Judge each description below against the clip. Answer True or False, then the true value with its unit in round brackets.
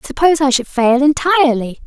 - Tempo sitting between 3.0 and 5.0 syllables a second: False (5.9 syllables/s)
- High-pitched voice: True (280 Hz)